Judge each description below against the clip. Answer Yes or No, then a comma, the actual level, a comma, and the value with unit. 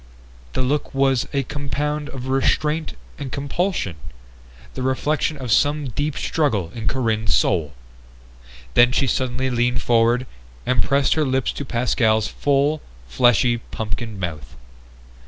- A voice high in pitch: No, low, 130 Hz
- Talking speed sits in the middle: No, slow, 130 wpm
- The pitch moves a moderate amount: Yes, average, 3.6 semitones